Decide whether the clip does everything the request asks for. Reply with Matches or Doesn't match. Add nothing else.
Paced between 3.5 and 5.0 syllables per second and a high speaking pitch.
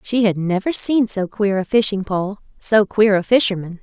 Matches